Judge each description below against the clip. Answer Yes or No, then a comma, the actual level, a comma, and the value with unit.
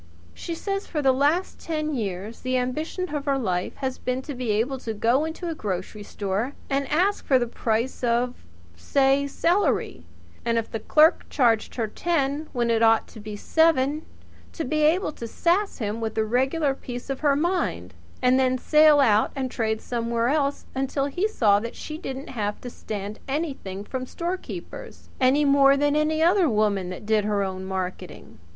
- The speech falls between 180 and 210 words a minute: Yes, average, 185 wpm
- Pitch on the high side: Yes, very high, 260 Hz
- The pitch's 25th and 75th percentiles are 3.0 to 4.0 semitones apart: No, wide, 5.4 semitones